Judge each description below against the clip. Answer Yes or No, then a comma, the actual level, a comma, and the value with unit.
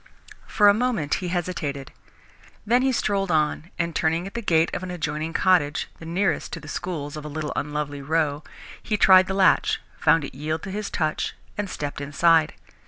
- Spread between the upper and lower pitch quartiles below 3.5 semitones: No, average, 3.9 semitones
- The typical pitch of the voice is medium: Yes, medium, 165 Hz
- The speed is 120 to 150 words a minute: No, average, 190 wpm